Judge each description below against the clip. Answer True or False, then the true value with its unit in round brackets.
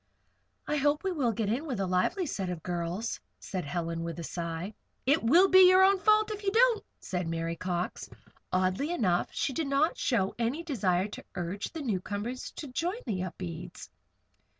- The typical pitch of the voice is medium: False (220 Hz)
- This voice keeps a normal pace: True (185 wpm)